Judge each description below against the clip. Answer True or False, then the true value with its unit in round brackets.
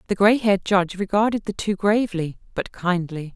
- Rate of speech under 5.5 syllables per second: False (5.7 syllables/s)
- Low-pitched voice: False (195 Hz)